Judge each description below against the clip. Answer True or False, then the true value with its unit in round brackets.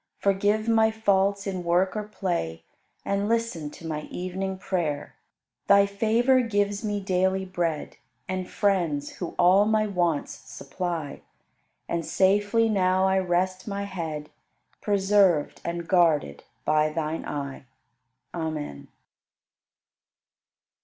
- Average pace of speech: False (115 wpm)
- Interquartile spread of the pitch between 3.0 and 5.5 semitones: True (3.5 semitones)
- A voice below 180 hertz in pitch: False (185 Hz)